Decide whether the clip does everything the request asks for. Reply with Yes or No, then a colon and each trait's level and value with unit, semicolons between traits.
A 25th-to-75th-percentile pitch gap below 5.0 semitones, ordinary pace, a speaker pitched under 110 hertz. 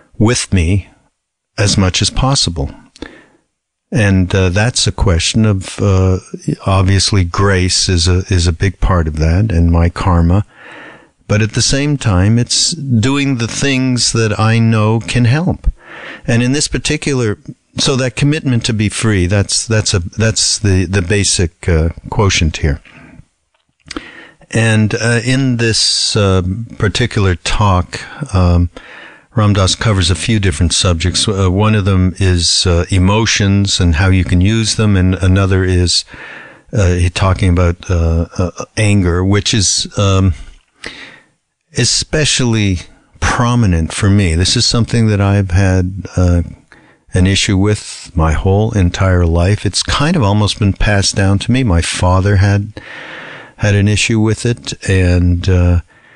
Yes: average, 3.5 semitones; average, 145 wpm; low, 100 Hz